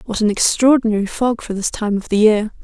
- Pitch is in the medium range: No, high, 215 Hz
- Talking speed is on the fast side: Yes, fast, 225 wpm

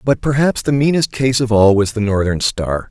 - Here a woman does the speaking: No, male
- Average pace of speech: No, fast, 225 wpm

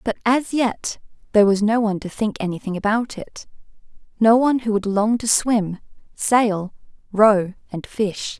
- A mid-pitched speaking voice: No, high, 215 Hz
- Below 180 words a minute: Yes, average, 165 wpm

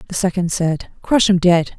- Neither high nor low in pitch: Yes, medium, 180 Hz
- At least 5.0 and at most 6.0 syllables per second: No, 4.8 syllables/s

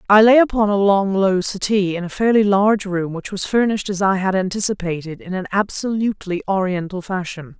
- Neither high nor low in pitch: No, high, 195 Hz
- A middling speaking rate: Yes, average, 190 wpm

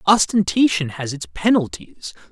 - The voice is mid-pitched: Yes, medium, 180 Hz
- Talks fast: No, slow, 105 wpm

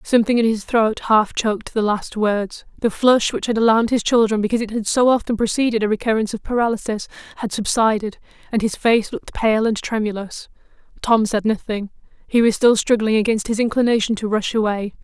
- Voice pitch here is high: Yes, high, 220 Hz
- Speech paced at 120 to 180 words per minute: No, average, 190 wpm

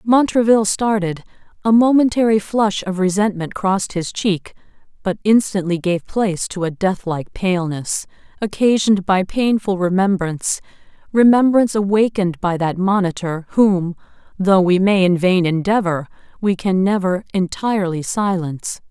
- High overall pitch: Yes, high, 195 Hz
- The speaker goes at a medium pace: No, slow, 125 wpm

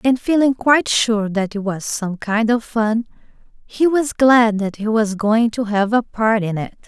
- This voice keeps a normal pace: No, fast, 210 wpm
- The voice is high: Yes, high, 225 Hz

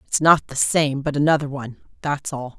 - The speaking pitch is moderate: Yes, medium, 145 Hz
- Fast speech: Yes, fast, 210 wpm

